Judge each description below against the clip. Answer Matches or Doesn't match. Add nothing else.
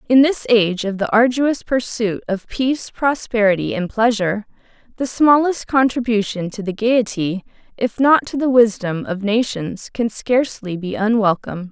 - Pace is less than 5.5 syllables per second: Matches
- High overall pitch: Matches